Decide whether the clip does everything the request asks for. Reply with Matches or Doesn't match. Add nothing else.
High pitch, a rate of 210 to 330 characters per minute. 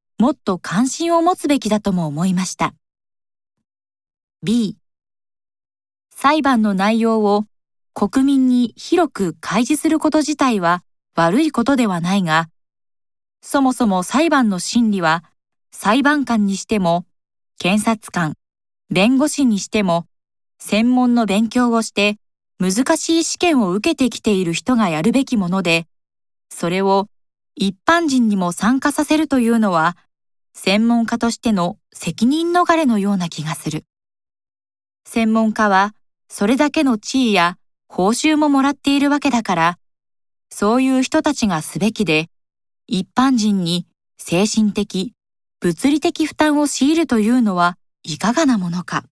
Matches